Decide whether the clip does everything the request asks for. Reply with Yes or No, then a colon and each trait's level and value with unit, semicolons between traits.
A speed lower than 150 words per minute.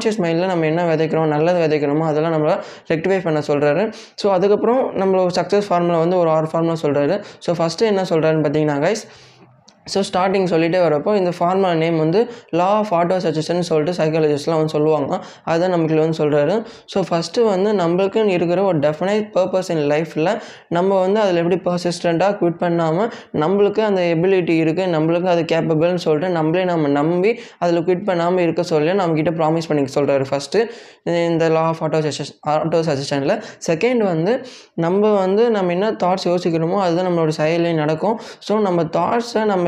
No: fast, 165 wpm